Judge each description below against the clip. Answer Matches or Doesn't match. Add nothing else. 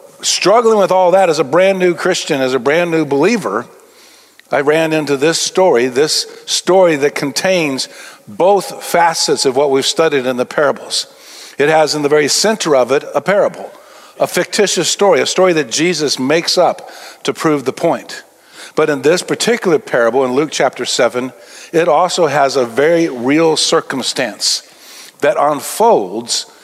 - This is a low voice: Doesn't match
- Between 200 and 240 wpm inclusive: Doesn't match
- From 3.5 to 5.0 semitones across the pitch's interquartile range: Matches